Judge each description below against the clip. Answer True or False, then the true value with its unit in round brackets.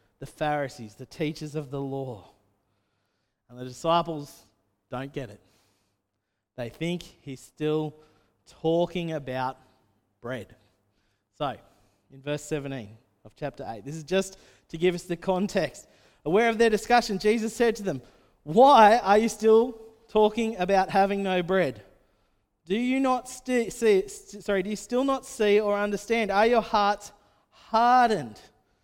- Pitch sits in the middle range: True (155 Hz)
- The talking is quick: False (145 wpm)